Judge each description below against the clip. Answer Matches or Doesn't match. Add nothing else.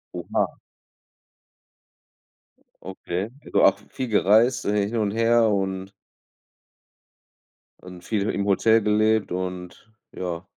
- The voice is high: Doesn't match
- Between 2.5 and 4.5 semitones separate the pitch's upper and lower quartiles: Matches